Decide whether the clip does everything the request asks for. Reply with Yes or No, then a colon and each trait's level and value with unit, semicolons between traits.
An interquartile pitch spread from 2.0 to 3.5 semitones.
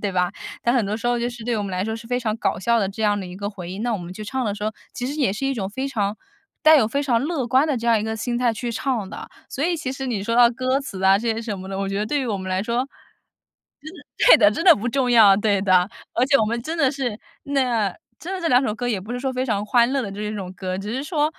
No: average, 4.2 semitones